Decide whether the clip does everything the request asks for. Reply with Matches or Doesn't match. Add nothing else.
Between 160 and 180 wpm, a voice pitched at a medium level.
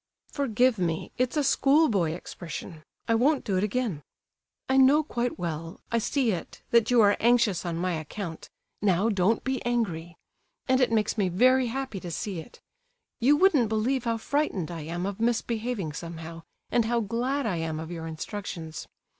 Doesn't match